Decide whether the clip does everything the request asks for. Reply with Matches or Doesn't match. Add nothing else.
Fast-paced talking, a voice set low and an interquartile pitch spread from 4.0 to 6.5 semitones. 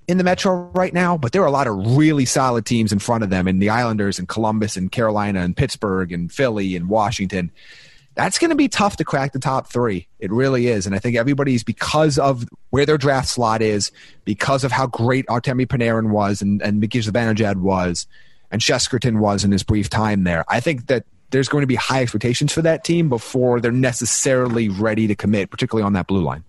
Matches